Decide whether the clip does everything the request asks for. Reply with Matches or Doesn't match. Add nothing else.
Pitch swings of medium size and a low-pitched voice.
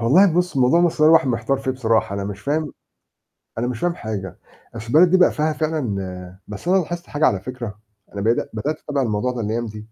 Doesn't match